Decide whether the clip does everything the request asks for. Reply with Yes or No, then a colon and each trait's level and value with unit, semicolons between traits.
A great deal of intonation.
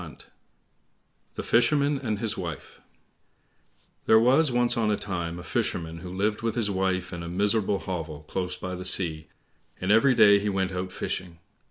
No: average, 3.7 semitones